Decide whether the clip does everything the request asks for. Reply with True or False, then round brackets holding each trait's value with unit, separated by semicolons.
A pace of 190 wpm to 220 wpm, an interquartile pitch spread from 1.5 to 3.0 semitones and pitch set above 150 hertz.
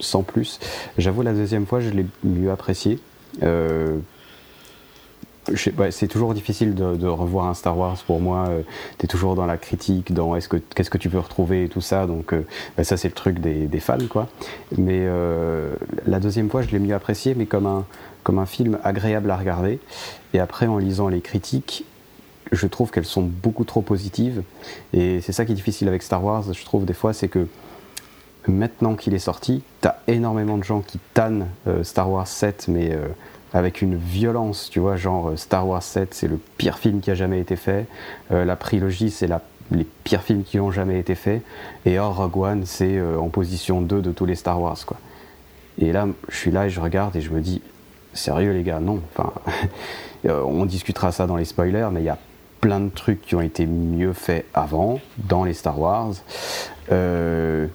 False (210 wpm; 2.7 semitones; 95 Hz)